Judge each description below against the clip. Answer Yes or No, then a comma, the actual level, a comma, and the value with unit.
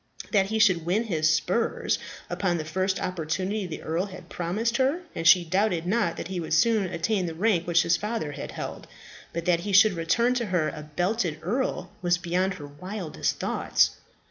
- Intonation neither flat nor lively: Yes, average, 4.1 semitones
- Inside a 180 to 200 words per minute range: Yes, average, 195 wpm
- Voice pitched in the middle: Yes, medium, 180 Hz